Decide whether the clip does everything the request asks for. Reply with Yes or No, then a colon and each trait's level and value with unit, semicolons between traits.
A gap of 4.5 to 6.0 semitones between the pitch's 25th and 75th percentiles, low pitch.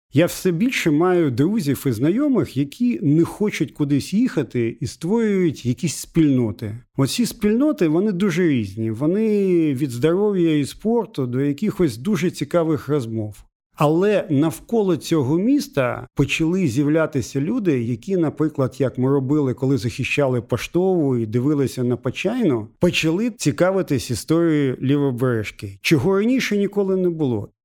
No: wide, 5.6 semitones; medium, 150 Hz